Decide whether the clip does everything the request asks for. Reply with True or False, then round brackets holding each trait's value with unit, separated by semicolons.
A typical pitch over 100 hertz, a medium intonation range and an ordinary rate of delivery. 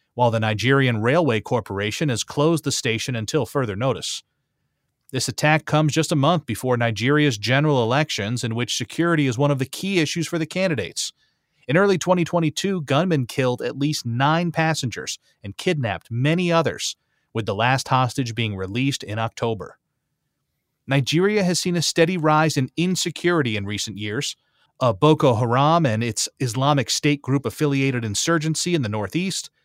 True (140 Hz; 4.9 semitones; 160 wpm)